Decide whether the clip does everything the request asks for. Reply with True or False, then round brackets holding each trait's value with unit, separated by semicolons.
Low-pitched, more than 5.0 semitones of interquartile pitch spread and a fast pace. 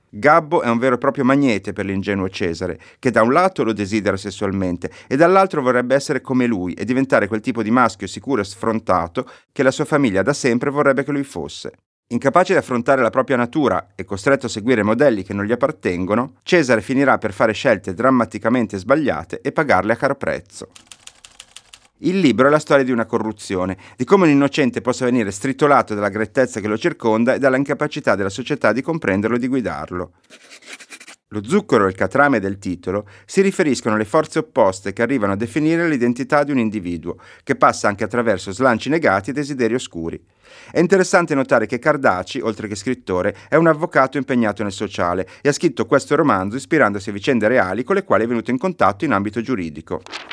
True (120 Hz; 5.4 semitones; 190 wpm)